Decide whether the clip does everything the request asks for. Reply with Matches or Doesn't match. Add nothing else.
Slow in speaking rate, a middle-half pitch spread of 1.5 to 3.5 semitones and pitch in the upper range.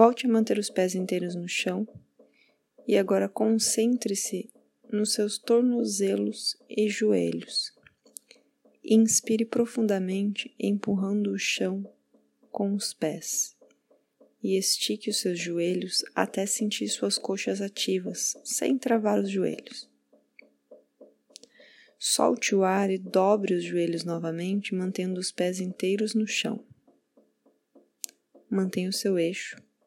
Matches